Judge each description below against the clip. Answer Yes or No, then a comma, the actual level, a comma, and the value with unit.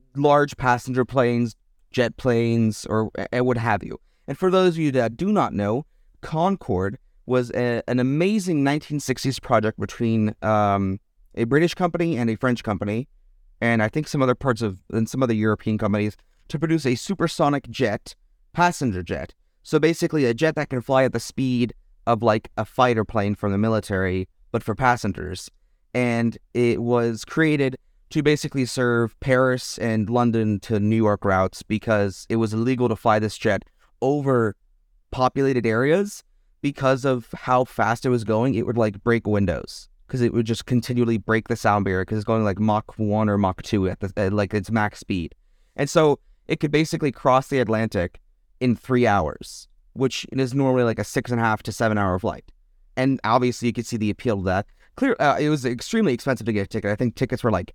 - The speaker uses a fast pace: No, average, 185 wpm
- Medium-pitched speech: No, low, 115 Hz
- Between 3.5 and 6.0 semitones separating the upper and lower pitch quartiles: Yes, average, 3.8 semitones